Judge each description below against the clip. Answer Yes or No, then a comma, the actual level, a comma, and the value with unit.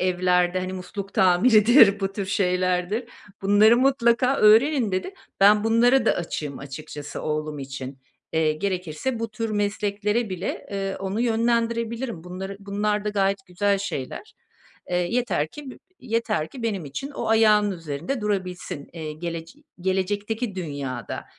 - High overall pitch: Yes, high, 200 Hz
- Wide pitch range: No, average, 4.1 semitones